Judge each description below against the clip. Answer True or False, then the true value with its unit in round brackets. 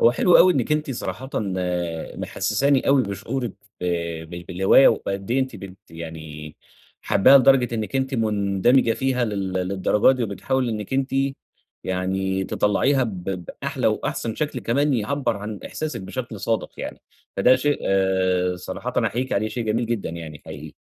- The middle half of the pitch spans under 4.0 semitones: False (5.5 semitones)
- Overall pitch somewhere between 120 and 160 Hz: False (110 Hz)